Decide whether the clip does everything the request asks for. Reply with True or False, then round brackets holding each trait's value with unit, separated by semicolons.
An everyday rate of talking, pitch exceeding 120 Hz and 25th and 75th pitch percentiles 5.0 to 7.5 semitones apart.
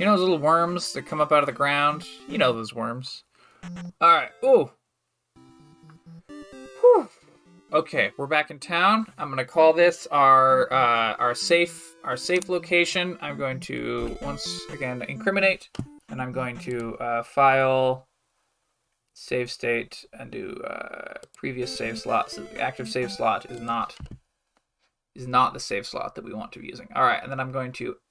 True (175 wpm; 135 Hz; 5.3 semitones)